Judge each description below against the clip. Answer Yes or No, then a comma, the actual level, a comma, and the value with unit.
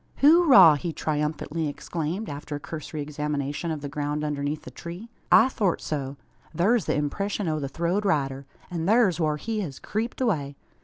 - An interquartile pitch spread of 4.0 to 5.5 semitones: Yes, average, 5.2 semitones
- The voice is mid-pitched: Yes, medium, 155 Hz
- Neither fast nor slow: Yes, average, 170 wpm